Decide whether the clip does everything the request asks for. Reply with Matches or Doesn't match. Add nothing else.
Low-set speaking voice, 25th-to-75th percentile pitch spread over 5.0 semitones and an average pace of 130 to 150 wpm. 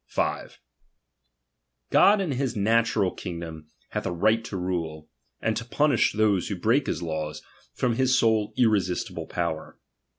Matches